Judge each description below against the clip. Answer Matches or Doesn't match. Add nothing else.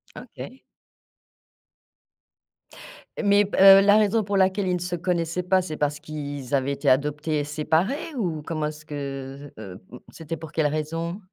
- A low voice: Doesn't match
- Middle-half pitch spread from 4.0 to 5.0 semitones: Matches